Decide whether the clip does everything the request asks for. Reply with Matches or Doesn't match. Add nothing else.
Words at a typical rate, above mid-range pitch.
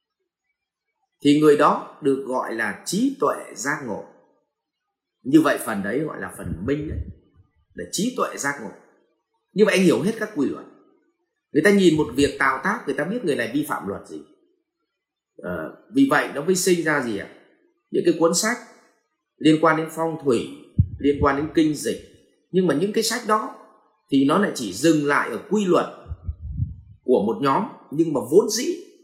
Matches